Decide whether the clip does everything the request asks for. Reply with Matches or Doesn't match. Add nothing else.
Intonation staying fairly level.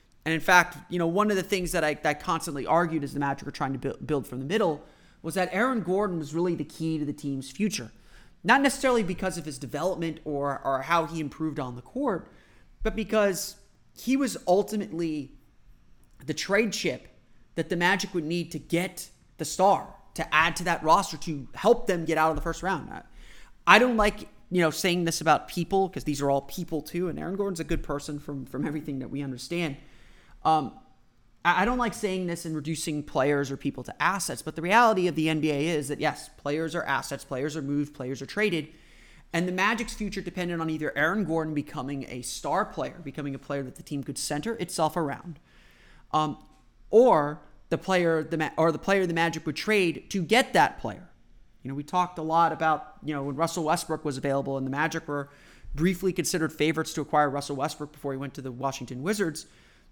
Doesn't match